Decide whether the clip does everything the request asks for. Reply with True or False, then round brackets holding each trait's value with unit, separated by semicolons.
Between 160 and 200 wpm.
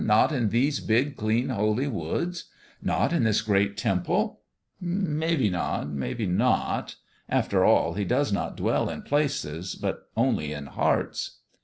False (150 wpm)